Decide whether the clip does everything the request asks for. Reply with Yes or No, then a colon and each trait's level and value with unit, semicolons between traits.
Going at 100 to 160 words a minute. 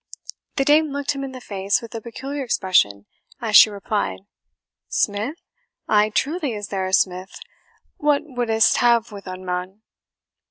Yes: average, 155 wpm